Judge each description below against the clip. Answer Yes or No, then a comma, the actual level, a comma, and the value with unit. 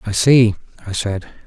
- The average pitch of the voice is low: Yes, low, 110 Hz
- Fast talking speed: No, average, 165 wpm